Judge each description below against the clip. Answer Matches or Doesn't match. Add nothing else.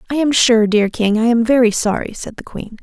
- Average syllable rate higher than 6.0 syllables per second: Doesn't match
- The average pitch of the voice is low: Doesn't match